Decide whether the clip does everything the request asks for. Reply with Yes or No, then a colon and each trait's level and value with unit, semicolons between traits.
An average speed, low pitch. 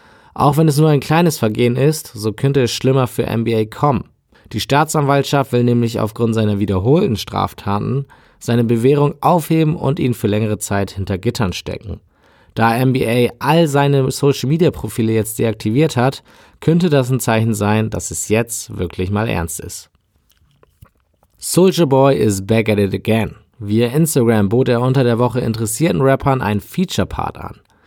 Yes: average, 165 wpm; low, 120 Hz